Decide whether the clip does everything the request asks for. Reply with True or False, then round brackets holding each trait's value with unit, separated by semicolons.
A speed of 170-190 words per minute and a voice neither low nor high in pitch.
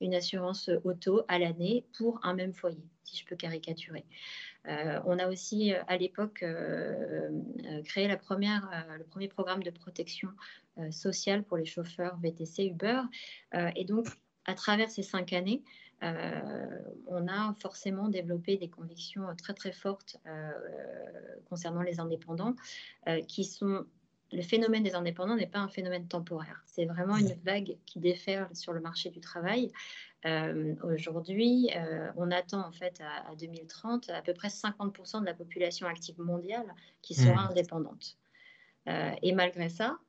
False (160 wpm; 180 Hz)